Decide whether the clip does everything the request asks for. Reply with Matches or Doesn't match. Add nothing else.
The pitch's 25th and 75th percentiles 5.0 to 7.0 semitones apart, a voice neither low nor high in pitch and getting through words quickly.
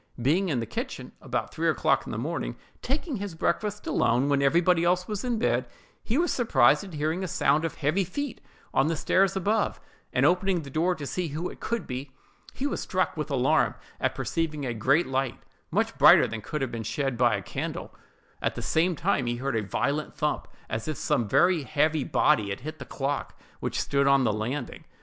Matches